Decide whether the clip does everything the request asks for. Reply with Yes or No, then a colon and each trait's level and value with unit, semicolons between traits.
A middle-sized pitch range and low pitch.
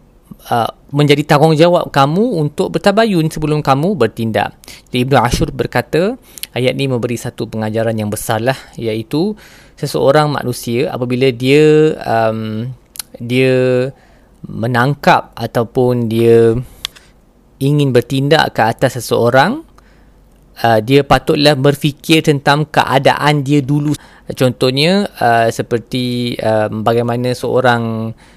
Yes: average, 4.1 semitones; low, 130 Hz